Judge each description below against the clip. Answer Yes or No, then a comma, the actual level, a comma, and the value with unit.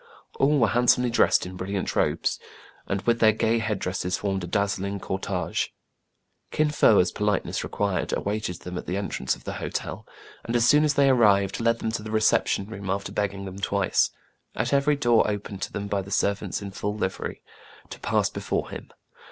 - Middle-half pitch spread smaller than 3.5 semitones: Yes, average, 3.0 semitones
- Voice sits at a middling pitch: No, low, 100 Hz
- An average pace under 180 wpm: No, average, 200 wpm